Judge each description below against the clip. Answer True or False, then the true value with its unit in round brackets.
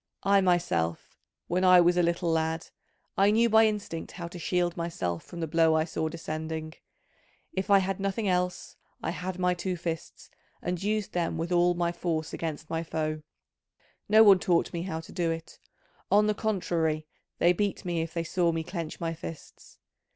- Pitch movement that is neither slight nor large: False (2.3 semitones)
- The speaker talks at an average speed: True (190 wpm)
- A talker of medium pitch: True (175 Hz)